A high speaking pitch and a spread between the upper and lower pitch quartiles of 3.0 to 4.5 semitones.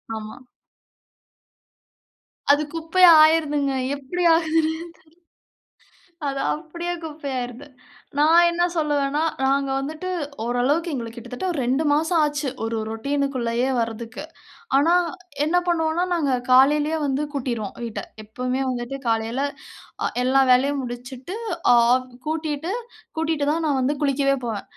Yes: very high, 280 Hz; average, 4.1 semitones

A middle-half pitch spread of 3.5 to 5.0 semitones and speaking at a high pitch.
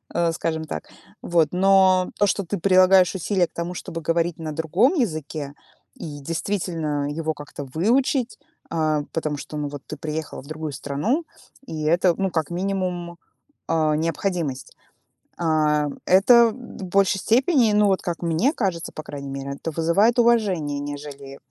No: average, 4.2 semitones; medium, 170 Hz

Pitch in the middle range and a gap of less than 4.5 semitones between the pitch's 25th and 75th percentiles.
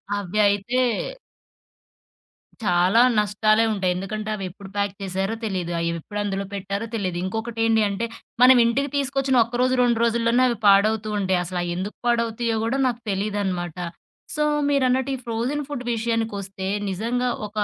No: high, 215 Hz; average, 3.4 semitones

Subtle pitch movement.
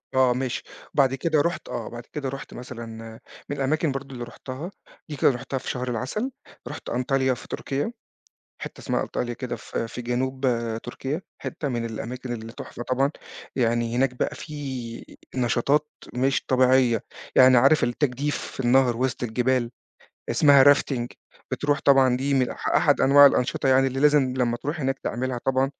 Yes: narrow, 2.2 semitones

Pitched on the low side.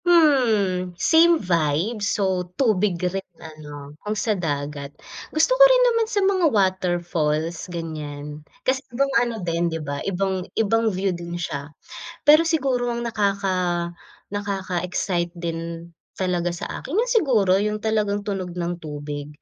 No: medium, 185 Hz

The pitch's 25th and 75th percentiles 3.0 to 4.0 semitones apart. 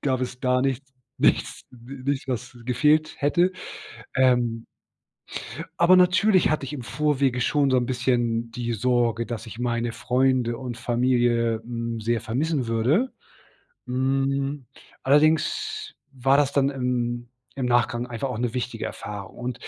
No: narrow, 2.6 semitones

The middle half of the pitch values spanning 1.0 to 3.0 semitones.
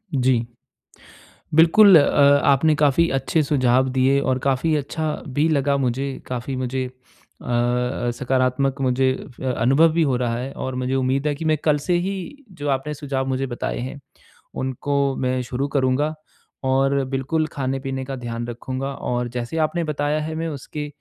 Yes: average, 2.7 semitones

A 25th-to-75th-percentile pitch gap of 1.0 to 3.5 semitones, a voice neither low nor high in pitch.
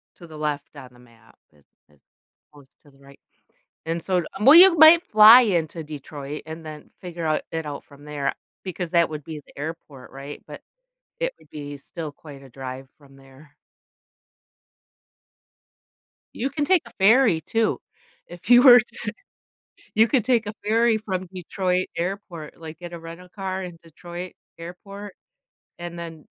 No: wide, 5.5 semitones; medium, 170 Hz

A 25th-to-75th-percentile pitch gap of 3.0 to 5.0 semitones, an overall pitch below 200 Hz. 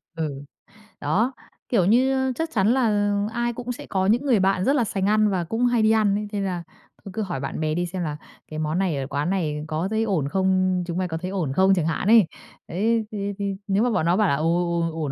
Yes: average, 4.5 semitones; high, 190 Hz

